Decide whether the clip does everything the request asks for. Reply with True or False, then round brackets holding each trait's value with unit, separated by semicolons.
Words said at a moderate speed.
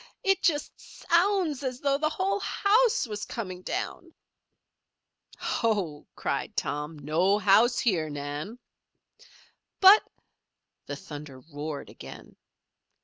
False (120 wpm)